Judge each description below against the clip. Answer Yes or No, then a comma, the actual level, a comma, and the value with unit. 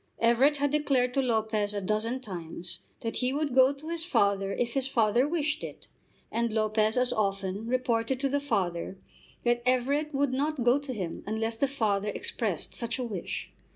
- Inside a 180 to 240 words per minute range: Yes, average, 185 wpm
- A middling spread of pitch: Yes, average, 4.3 semitones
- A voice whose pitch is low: No, high, 240 Hz